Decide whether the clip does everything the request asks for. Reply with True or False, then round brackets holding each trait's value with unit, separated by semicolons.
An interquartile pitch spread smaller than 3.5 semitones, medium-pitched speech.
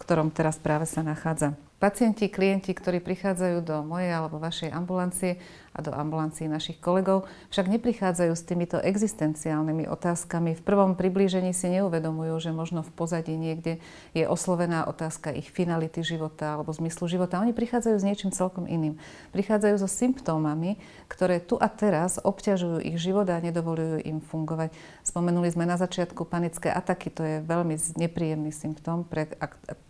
True (2.6 semitones; 170 Hz)